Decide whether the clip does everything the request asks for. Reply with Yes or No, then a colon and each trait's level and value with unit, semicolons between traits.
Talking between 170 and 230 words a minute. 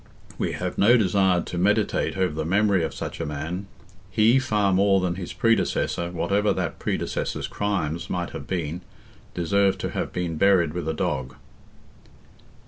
No: average, 160 wpm